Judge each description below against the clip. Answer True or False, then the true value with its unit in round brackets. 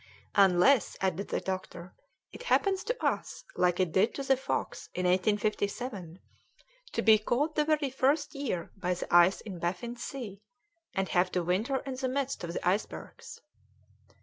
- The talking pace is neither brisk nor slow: True (165 wpm)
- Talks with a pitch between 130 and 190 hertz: False (205 Hz)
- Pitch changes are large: True (6.7 semitones)